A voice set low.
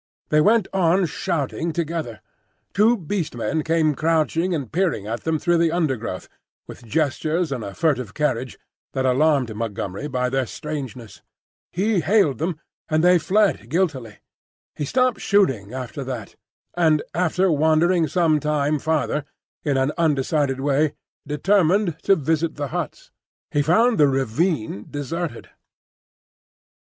No: medium, 155 Hz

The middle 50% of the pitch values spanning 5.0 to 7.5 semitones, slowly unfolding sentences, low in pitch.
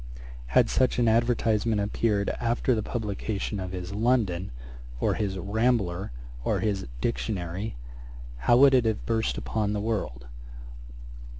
No: average, 3.2 semitones; slow, 130 wpm; low, 105 Hz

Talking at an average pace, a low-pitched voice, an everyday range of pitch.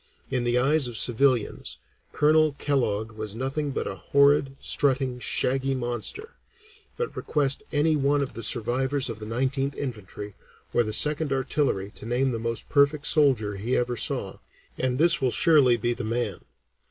Yes: average, 165 wpm; low, 130 Hz; average, 3.4 semitones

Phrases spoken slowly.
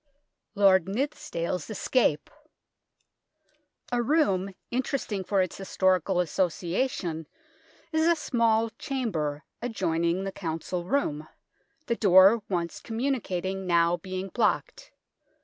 Yes: slow, 105 wpm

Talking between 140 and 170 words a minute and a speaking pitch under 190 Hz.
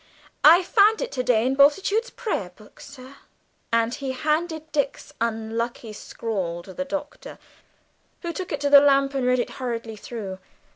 No: average, 160 wpm; very high, 270 Hz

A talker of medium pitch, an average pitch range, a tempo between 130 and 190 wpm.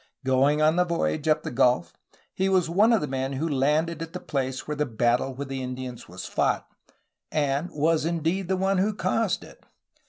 No: medium, 150 Hz; average, 4.5 semitones; average, 200 wpm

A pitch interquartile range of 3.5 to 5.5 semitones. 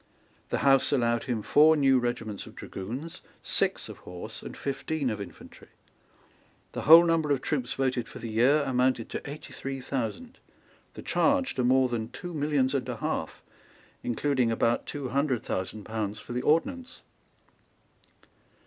Yes: average, 3.9 semitones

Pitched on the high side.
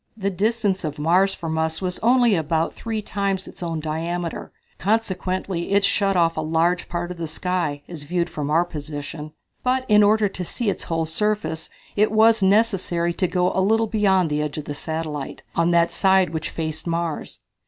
No: medium, 175 Hz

